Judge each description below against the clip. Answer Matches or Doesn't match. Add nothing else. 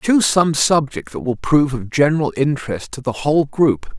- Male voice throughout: Matches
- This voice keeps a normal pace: Matches